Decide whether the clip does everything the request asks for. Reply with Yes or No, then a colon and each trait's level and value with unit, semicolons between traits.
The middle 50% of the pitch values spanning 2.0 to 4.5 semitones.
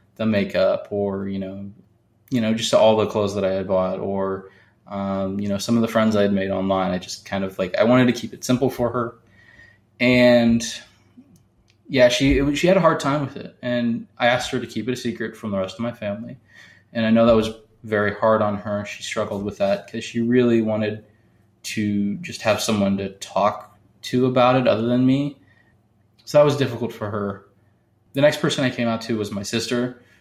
Yes: average, 3.2 semitones